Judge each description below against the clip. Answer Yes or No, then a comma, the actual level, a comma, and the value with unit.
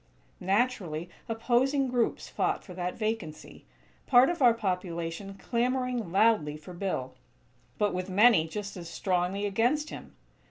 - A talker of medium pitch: No, high, 200 Hz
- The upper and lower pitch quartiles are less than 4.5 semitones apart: No, average, 5.2 semitones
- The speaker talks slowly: Yes, slow, 130 wpm